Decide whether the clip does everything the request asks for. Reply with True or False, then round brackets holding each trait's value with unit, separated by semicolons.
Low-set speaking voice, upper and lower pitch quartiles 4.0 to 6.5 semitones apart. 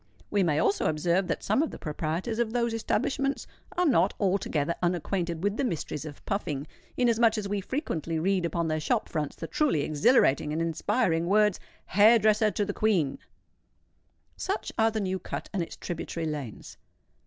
False (190 Hz; 5.2 semitones)